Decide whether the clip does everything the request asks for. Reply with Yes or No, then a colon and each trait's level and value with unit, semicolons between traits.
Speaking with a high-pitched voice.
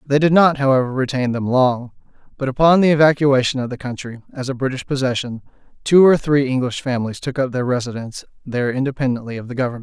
No: low, 130 Hz